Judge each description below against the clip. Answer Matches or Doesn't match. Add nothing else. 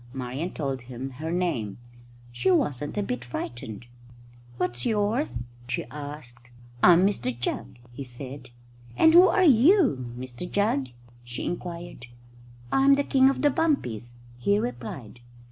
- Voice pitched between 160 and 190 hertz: Doesn't match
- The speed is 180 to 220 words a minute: Doesn't match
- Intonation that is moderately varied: Doesn't match